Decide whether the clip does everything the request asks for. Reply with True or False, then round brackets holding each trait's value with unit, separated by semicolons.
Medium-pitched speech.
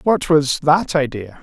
True (150 Hz)